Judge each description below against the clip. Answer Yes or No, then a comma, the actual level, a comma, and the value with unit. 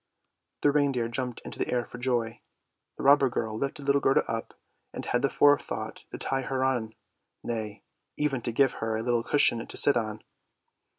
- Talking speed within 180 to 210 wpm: Yes, average, 190 wpm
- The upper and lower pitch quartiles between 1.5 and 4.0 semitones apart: Yes, average, 3.2 semitones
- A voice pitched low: Yes, low, 125 Hz